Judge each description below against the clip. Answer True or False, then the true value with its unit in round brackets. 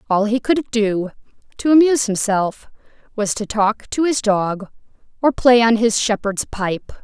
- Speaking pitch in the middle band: False (225 Hz)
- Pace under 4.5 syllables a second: True (4.3 syllables/s)